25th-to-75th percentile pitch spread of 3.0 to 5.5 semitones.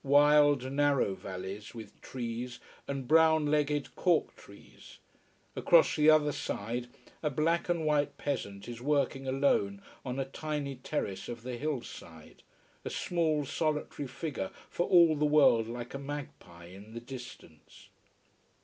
Yes: average, 4.1 semitones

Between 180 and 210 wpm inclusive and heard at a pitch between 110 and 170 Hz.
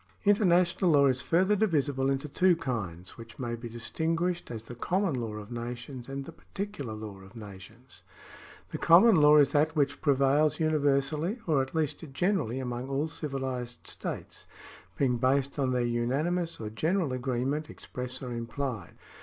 No: average, 160 wpm; low, 135 Hz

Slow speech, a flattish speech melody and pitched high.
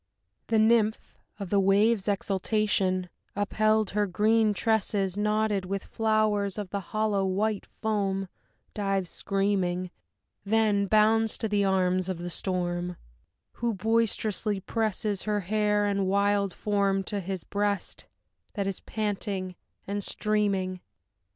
Yes: slow, 125 wpm; narrow, 1.9 semitones; high, 205 Hz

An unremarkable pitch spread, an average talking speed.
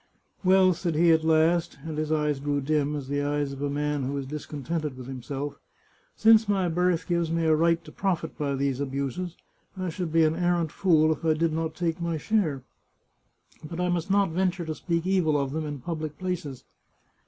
No: average, 3.0 semitones; fast, 210 wpm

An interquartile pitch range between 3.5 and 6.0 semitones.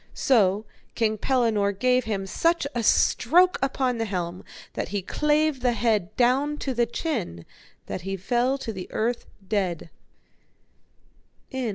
Yes: average, 4.8 semitones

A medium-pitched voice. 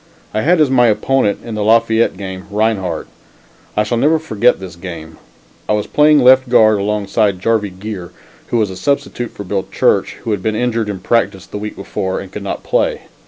No: low, 105 Hz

